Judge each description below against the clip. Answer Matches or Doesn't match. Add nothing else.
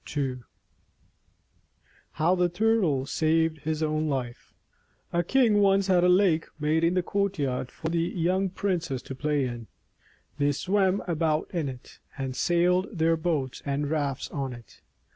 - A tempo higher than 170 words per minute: Doesn't match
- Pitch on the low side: Doesn't match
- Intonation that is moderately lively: Matches